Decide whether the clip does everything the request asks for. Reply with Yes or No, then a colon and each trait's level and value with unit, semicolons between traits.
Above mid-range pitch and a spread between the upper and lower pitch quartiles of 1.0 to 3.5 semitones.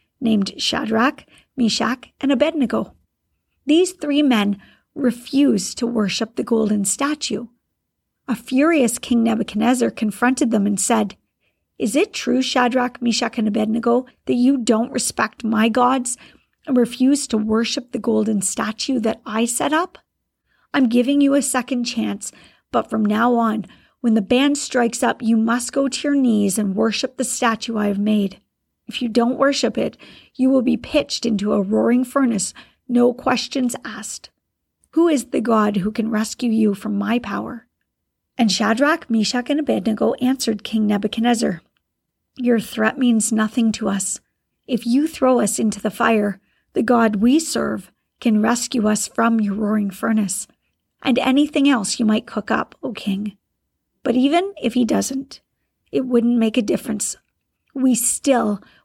Yes: high, 235 Hz; average, 2.9 semitones